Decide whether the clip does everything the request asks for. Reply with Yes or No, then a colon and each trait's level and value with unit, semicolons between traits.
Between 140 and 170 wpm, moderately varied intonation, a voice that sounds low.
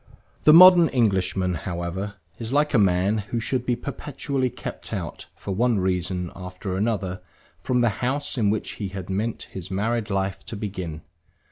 Yes: average, 165 wpm; average, 4.5 semitones; low, 100 Hz